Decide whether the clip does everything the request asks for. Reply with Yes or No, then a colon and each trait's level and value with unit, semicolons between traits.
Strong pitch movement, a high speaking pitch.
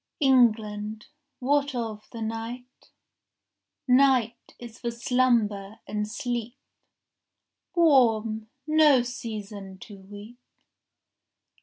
No: average, 2.9 semitones; high, 230 Hz